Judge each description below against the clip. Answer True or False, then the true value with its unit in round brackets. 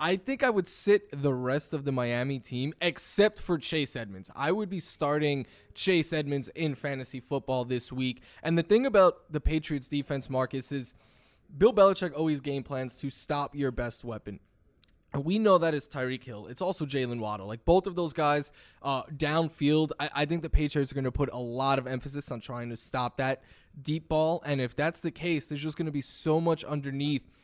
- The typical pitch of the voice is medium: True (145 Hz)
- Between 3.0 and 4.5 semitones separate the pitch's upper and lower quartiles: True (3.8 semitones)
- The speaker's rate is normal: False (210 wpm)